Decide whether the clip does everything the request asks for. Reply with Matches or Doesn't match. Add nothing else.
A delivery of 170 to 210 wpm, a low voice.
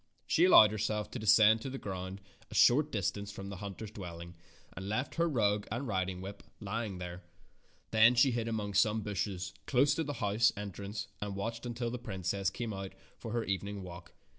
Matches